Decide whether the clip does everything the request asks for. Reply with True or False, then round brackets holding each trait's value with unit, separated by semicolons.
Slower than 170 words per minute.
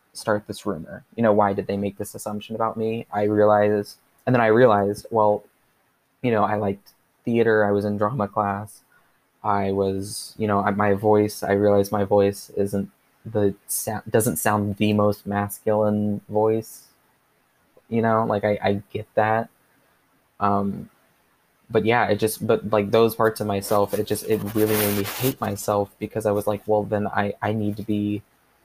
False (185 wpm)